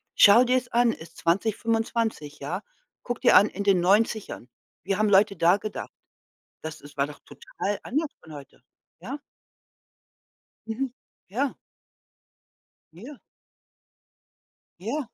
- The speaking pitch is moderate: No, high, 205 Hz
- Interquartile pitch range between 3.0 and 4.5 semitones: No, average, 5.2 semitones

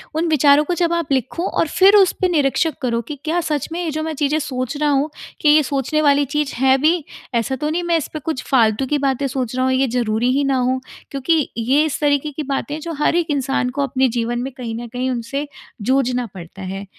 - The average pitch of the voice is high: Yes, very high, 275 Hz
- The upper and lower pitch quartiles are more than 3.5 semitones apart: No, average, 3.2 semitones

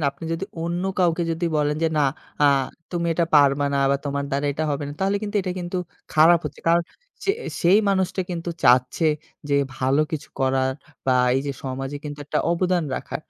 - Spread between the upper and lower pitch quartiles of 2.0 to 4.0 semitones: Yes, average, 3.7 semitones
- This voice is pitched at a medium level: Yes, medium, 155 Hz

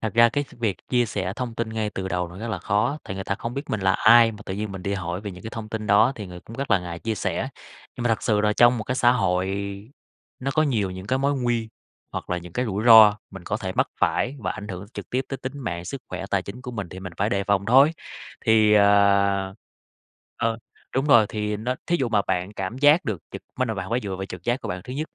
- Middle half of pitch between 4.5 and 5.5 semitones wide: No, average, 3.9 semitones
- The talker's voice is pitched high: No, low, 105 Hz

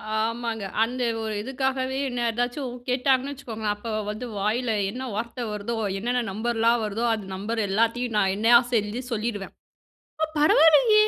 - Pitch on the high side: Yes, high, 235 Hz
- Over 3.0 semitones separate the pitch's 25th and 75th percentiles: No, average, 2.7 semitones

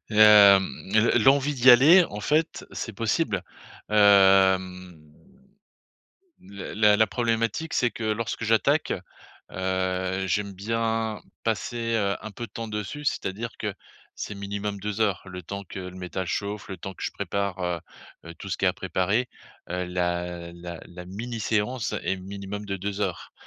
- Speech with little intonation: No, average, 3.2 semitones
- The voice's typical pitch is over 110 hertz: No, low, 100 Hz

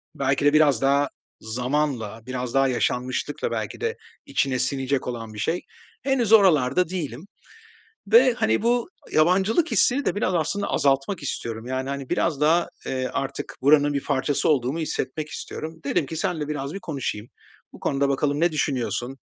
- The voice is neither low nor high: Yes, medium, 145 Hz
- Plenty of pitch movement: No, average, 4.3 semitones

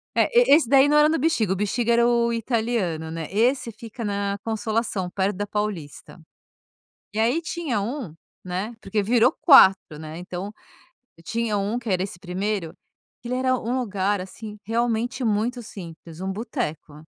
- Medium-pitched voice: No, high, 215 Hz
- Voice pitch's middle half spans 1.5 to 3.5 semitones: No, average, 4.0 semitones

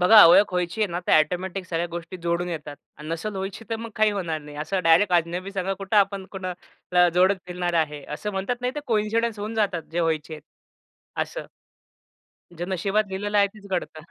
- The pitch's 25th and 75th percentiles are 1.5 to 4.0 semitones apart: Yes, average, 3.2 semitones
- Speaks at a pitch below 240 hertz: Yes, medium, 185 Hz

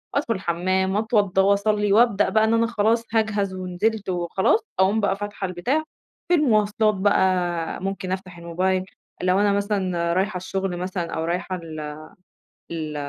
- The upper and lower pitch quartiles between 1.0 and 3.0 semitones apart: Yes, narrow, 2.6 semitones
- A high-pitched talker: Yes, high, 195 Hz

